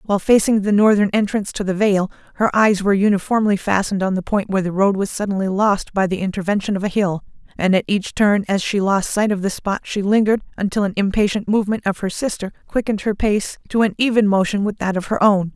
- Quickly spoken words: Yes, fast, 230 wpm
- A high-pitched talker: Yes, high, 200 Hz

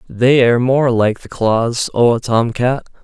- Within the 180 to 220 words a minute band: Yes, average, 200 wpm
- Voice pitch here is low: Yes, low, 120 Hz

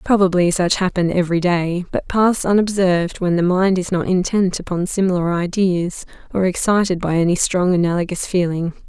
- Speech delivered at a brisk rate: No, average, 160 wpm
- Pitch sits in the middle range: Yes, medium, 180 Hz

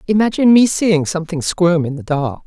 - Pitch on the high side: No, medium, 175 Hz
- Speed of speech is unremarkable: Yes, average, 195 wpm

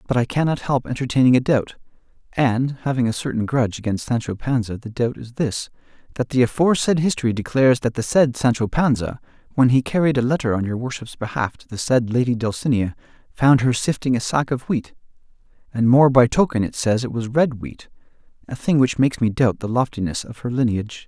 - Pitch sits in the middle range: No, low, 125 Hz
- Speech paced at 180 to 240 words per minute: Yes, average, 200 wpm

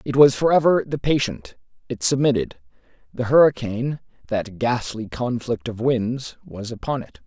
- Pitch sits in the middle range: No, low, 125 Hz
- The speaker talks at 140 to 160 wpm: Yes, average, 150 wpm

